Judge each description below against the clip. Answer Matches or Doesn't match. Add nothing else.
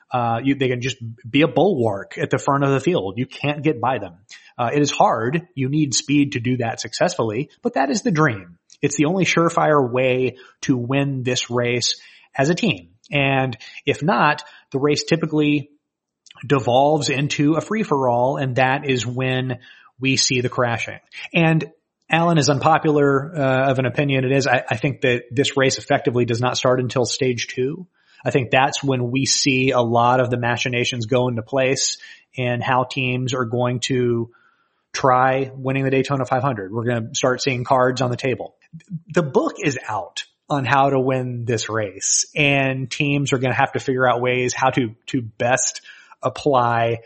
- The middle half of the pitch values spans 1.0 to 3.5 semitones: Matches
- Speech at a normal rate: Matches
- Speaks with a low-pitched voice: Matches